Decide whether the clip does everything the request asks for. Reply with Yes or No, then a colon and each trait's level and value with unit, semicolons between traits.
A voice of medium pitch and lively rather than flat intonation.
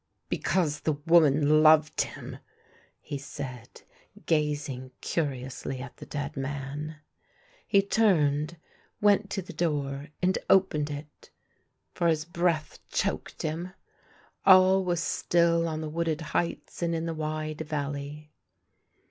No: medium, 155 Hz; average, 2.8 semitones